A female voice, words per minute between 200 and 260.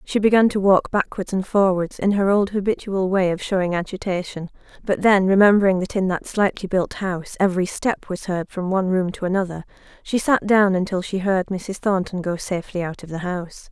Yes: female; fast, 205 wpm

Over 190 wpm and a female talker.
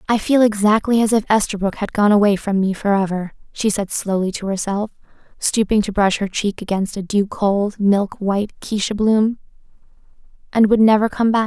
Yes: average, 200 wpm; female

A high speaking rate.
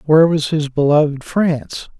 No: average, 150 wpm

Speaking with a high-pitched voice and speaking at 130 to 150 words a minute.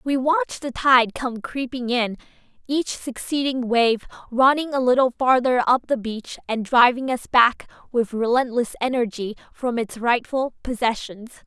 Yes: high, 245 Hz; average, 145 wpm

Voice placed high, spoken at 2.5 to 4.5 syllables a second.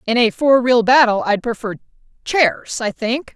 Yes: high, 235 Hz; 4.4 syllables/s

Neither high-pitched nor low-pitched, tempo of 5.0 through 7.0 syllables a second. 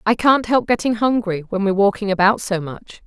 No: high, 205 Hz; 5.6 syllables/s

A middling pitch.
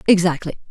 Yes: medium, 175 Hz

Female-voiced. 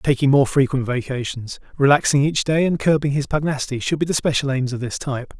No: male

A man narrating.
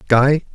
Yes: male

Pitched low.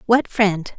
No: high, 205 Hz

